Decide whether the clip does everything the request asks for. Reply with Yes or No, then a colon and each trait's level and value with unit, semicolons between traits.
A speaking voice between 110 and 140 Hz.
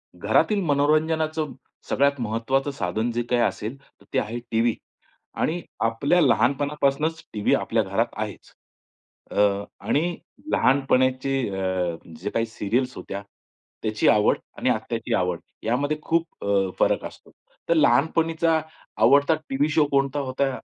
Yes: low, 135 Hz